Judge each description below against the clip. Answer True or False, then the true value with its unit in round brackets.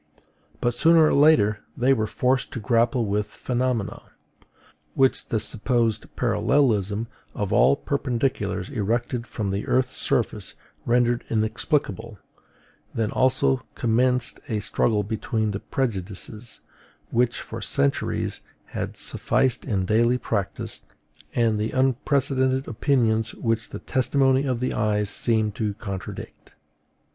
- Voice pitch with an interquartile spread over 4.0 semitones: False (3.3 semitones)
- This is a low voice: True (115 Hz)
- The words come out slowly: True (120 wpm)